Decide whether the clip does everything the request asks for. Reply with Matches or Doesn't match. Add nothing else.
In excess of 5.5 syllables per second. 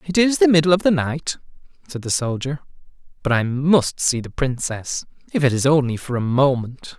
Doesn't match